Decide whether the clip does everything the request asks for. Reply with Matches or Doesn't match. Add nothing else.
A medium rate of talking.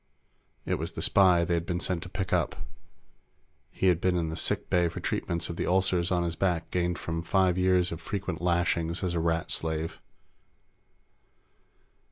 Matches